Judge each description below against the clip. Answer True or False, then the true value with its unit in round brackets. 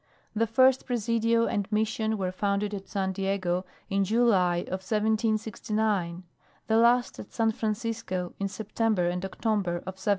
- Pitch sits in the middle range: False (210 Hz)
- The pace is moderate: True (145 wpm)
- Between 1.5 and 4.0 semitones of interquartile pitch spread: True (2.9 semitones)